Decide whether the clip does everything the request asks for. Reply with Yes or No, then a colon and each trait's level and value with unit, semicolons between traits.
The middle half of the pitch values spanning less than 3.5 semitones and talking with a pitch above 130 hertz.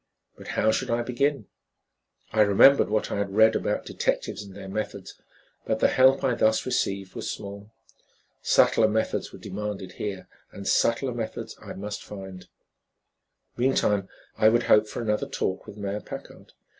No: average, 2.7 semitones; low, 105 Hz